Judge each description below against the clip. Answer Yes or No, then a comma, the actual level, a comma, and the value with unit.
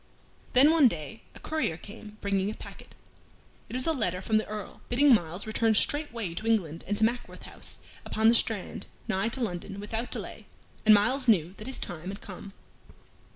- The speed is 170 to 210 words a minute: Yes, average, 190 wpm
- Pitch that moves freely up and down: No, average, 3.7 semitones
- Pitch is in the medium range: No, high, 215 Hz